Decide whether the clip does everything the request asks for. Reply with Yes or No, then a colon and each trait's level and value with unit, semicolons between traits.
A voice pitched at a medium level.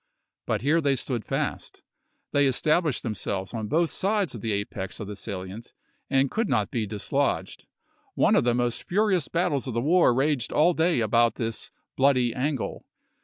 No: low, 125 Hz